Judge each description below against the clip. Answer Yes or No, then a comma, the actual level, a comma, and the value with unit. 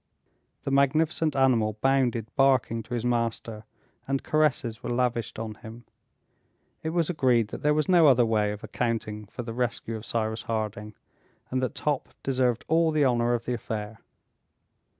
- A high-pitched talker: No, low, 120 Hz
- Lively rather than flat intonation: No, average, 3.4 semitones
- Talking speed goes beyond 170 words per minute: No, average, 165 wpm